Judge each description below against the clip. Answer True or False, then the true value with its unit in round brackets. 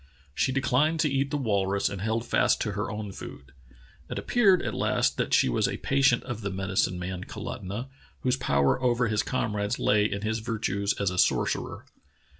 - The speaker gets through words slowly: False (195 wpm)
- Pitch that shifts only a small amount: False (4.4 semitones)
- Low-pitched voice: True (110 Hz)